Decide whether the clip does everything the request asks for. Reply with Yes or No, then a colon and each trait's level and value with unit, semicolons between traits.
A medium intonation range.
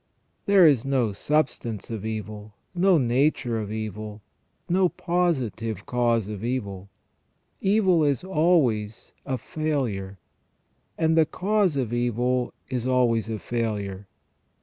No: wide, 6.3 semitones